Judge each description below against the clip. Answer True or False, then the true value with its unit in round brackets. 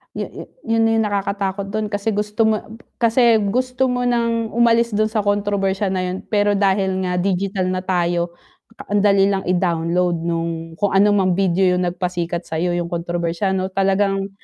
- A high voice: True (195 Hz)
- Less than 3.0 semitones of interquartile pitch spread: True (2.6 semitones)